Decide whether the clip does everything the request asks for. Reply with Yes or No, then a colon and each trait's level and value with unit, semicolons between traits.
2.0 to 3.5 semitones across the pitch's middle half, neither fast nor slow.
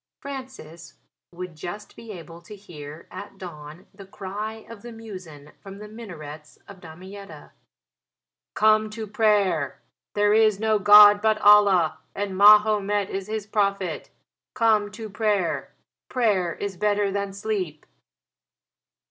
No: average, 2.8 semitones; slow, 130 wpm